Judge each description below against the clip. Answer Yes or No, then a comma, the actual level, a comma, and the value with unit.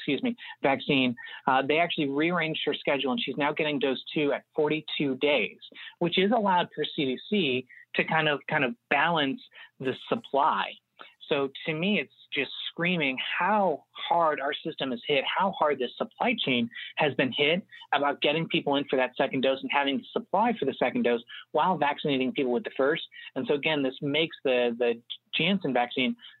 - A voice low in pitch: No, medium, 145 Hz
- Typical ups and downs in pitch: Yes, average, 4.0 semitones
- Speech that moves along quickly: Yes, fast, 185 wpm